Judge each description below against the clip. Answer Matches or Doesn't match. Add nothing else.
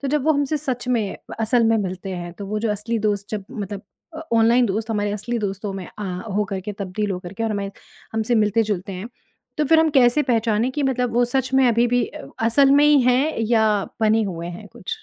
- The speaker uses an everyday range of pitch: Matches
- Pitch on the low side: Doesn't match